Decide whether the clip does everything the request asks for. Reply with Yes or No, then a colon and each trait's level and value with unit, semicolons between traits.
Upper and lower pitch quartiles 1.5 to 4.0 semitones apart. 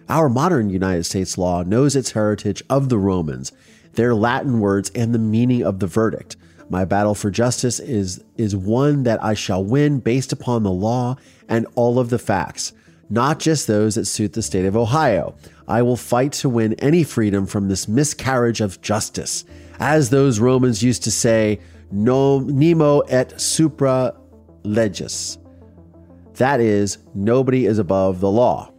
No: average, 4.5 semitones